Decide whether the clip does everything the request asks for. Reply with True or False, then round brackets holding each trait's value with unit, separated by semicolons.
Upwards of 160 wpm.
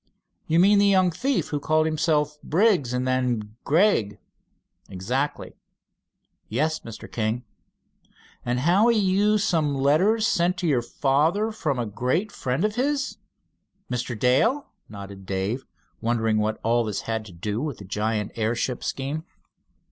False (145 wpm)